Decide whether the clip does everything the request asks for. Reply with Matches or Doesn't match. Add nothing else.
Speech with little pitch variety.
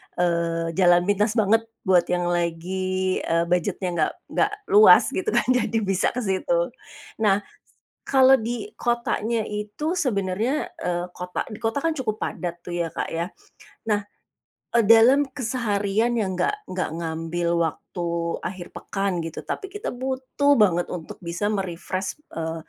Doesn't match